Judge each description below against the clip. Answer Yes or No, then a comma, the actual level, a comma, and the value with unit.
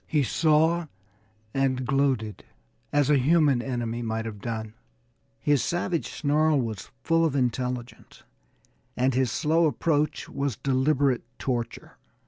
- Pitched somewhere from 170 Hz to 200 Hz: No, low, 135 Hz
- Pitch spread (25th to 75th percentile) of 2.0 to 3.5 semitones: No, average, 3.9 semitones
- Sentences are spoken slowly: Yes, slow, 120 wpm